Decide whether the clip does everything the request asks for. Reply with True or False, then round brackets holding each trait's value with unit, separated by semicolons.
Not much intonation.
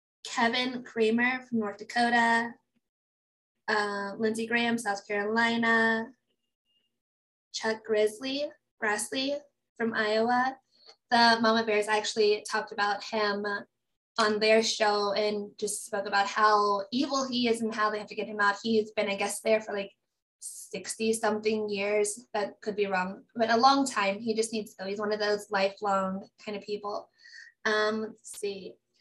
True (2.0 semitones)